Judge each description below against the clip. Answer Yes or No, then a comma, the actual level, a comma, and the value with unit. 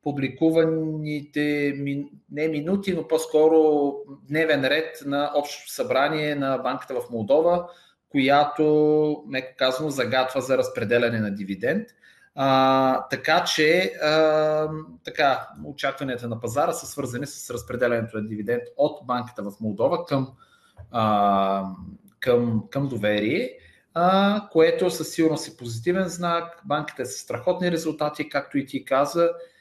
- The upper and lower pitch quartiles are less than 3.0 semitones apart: No, average, 3.8 semitones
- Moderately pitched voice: Yes, medium, 145 Hz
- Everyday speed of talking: Yes, average, 125 wpm